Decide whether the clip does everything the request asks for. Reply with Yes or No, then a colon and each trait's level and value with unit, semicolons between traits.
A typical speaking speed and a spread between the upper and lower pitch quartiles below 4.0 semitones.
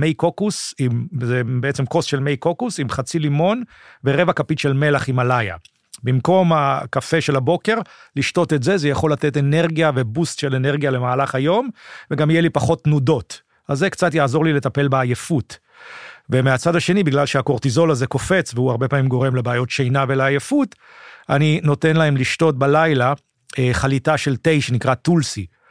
No: fast, 160 wpm; average, 3.5 semitones